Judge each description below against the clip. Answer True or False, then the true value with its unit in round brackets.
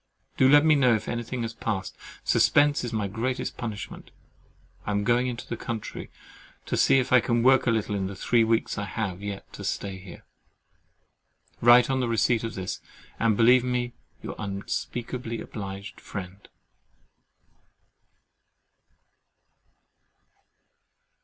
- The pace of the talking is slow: False (145 wpm)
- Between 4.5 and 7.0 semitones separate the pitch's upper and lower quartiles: False (3.3 semitones)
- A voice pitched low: True (115 Hz)